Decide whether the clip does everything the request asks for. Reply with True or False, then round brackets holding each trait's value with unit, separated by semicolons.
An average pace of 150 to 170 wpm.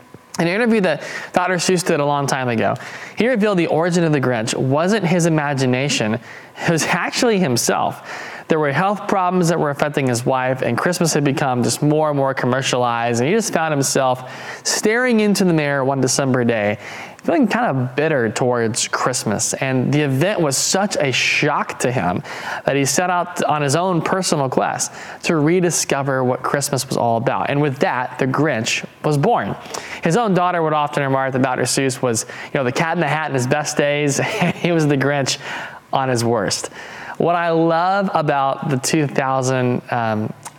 False (190 wpm)